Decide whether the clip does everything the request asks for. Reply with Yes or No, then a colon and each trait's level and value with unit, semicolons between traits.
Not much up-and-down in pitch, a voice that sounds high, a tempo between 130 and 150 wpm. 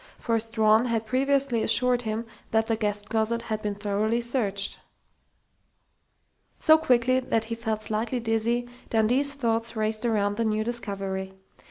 Yes: narrow, 1.8 semitones; high, 225 Hz; average, 145 wpm